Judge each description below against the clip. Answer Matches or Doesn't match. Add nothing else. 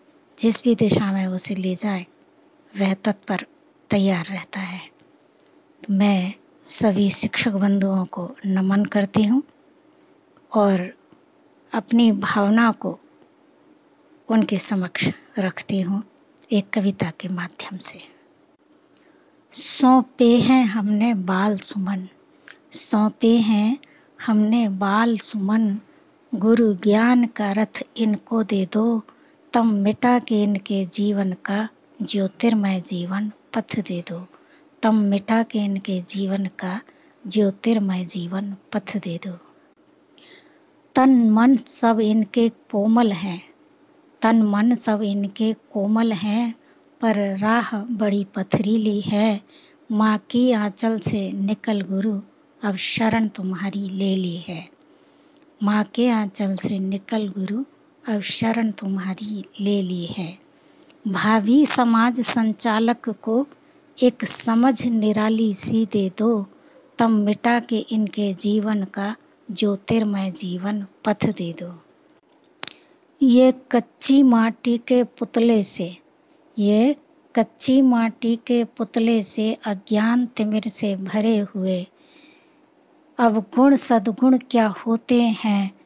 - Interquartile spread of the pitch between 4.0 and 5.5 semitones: Matches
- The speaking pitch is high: Matches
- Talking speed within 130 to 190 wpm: Doesn't match